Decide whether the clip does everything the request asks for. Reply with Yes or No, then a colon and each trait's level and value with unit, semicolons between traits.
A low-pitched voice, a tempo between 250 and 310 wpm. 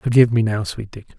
Yes: low, 110 Hz; fast, 255 wpm